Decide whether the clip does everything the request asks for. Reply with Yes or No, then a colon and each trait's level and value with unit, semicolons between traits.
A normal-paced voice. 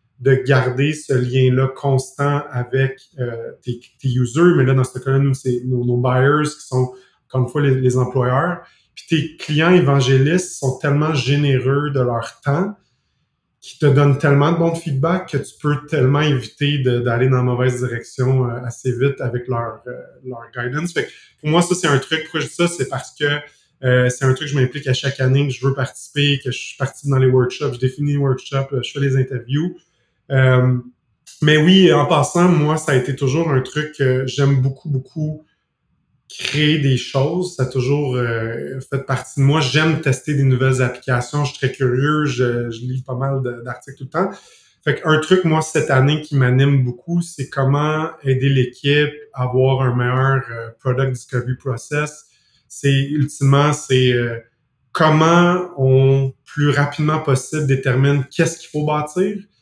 Yes: average, 190 wpm